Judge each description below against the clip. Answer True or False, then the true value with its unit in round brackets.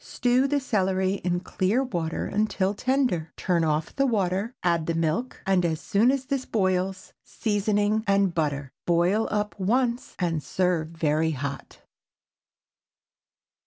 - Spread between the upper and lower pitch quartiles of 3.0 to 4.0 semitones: False (4.6 semitones)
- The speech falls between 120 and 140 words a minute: True (135 wpm)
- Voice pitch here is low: False (190 Hz)